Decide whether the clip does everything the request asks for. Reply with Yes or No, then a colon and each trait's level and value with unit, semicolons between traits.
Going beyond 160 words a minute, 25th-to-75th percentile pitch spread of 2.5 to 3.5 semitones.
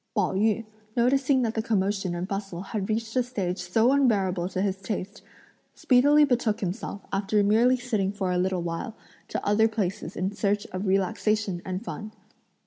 Yes: average, 170 wpm; average, 3.1 semitones